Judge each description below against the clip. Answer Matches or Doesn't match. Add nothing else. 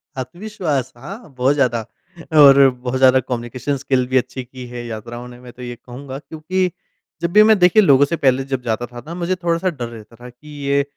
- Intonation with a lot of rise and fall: Doesn't match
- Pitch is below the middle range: Matches